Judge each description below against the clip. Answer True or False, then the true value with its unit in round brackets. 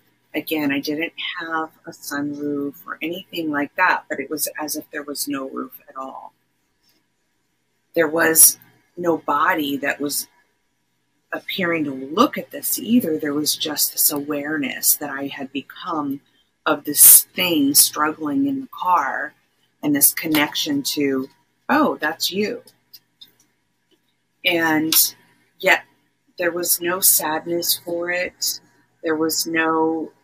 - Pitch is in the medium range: True (150 Hz)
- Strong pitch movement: False (3.0 semitones)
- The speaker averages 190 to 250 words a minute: False (135 wpm)